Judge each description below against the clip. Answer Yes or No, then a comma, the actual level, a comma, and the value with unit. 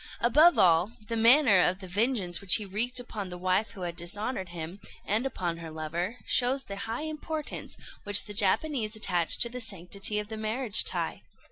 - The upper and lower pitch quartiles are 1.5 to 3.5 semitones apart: No, average, 4.8 semitones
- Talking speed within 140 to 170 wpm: No, average, 190 wpm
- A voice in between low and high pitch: No, high, 205 Hz